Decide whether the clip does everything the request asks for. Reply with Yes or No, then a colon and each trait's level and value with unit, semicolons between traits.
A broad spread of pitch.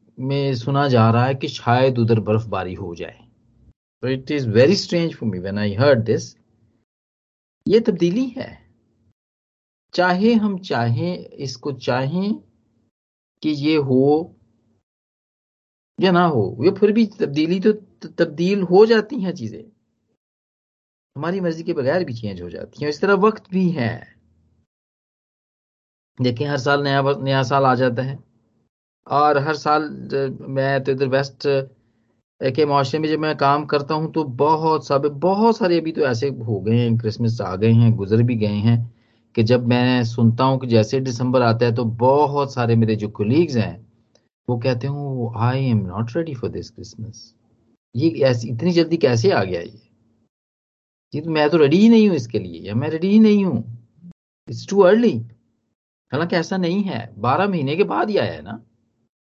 Yes: wide, 5.7 semitones